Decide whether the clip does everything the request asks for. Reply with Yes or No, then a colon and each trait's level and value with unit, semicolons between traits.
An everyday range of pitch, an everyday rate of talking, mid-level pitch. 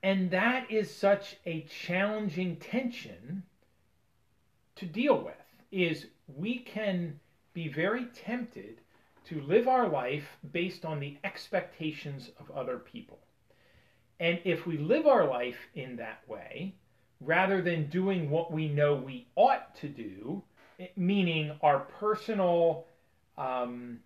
No: average, 5.0 semitones; slow, 125 wpm; medium, 170 Hz